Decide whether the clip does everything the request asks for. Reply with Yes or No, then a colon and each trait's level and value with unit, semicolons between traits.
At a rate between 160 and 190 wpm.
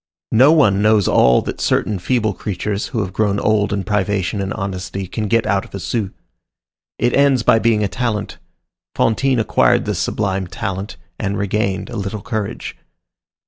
Yes: average, 170 wpm